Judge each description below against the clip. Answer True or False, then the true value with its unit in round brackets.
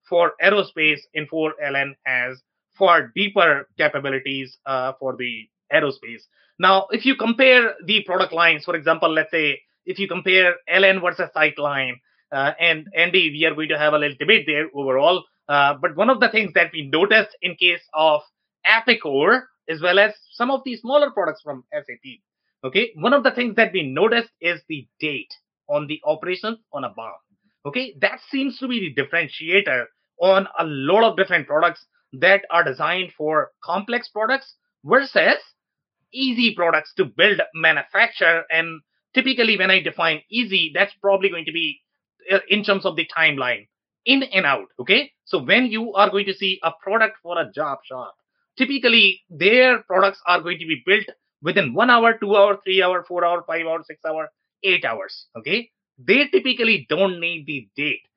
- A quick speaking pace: False (175 wpm)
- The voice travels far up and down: True (5.8 semitones)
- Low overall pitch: False (180 Hz)